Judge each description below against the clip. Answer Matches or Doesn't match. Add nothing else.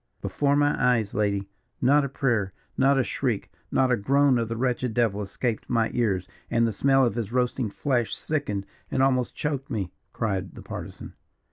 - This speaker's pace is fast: Doesn't match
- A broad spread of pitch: Doesn't match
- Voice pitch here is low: Matches